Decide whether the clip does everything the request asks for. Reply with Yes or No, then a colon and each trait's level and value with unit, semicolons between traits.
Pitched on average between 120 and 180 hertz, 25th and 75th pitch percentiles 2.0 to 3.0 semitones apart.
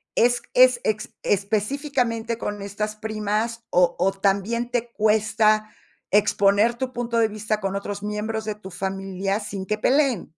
No: high, 215 Hz; narrow, 2.5 semitones